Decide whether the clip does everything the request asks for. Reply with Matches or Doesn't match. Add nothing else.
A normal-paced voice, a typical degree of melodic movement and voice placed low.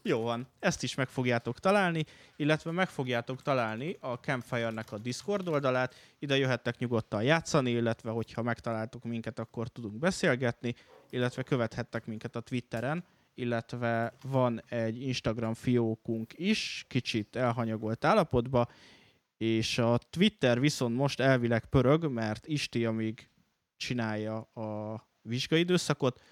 Matches